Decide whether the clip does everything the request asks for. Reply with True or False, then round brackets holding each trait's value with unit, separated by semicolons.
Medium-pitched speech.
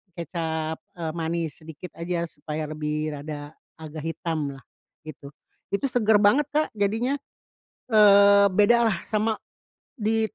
True (170 Hz)